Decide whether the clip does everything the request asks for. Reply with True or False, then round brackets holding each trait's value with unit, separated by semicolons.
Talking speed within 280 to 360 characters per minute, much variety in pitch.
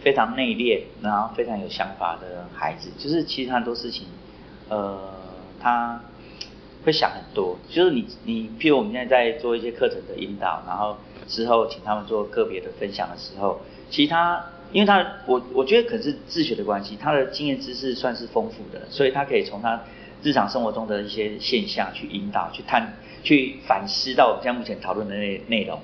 True (300 characters per minute; 8.3 semitones)